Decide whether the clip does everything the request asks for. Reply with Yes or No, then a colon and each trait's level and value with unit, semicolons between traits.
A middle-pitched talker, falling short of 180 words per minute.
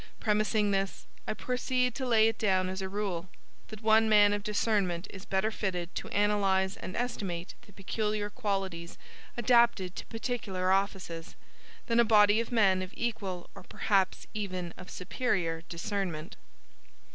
No: high, 200 Hz; average, 150 wpm